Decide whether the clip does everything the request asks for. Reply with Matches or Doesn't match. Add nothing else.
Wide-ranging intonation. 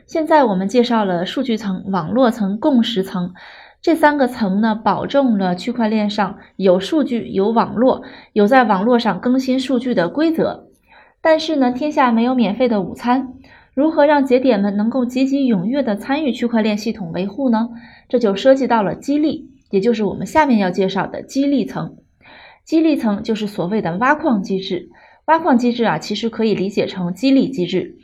Doesn't match